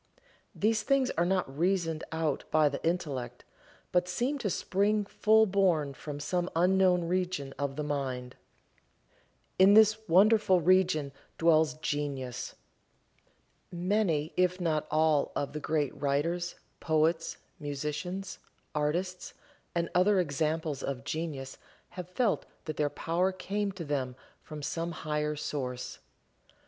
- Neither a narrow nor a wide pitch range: Yes, average, 4.0 semitones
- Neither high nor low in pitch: Yes, medium, 165 Hz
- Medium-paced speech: No, slow, 125 wpm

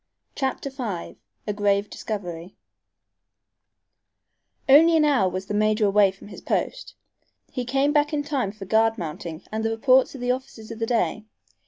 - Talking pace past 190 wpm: No, average, 165 wpm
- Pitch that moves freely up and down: No, average, 4.9 semitones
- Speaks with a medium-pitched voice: No, high, 225 Hz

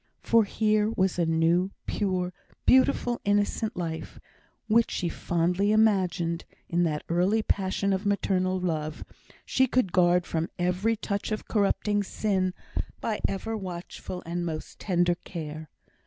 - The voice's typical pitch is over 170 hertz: Yes, medium, 185 Hz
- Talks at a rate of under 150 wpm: Yes, slow, 135 wpm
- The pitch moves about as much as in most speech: Yes, average, 3.3 semitones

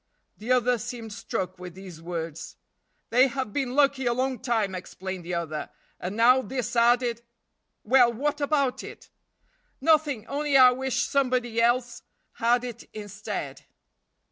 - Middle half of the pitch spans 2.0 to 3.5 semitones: No, average, 4.1 semitones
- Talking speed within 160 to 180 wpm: No, average, 145 wpm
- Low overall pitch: No, high, 240 Hz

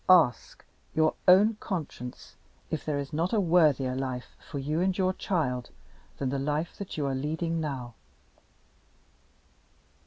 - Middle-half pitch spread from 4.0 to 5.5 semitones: Yes, average, 4.7 semitones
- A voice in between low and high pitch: Yes, medium, 155 Hz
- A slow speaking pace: No, average, 145 wpm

